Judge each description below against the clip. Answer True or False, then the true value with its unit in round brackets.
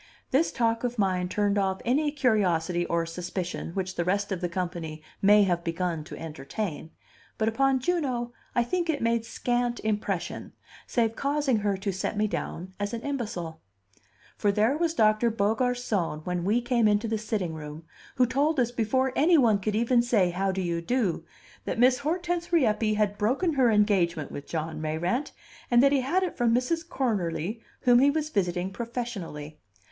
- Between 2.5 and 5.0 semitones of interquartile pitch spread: False (5.6 semitones)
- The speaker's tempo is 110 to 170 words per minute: False (180 wpm)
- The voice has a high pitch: True (215 Hz)